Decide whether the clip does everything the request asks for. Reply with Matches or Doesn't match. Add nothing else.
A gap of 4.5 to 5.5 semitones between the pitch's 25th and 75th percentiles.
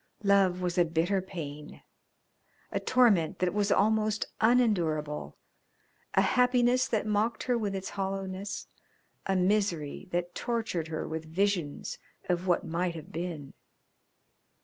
Doesn't match